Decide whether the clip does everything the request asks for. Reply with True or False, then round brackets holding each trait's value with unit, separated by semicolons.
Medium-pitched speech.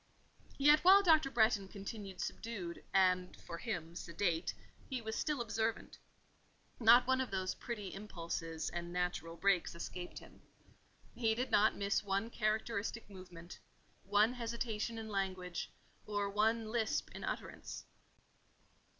False (205 Hz)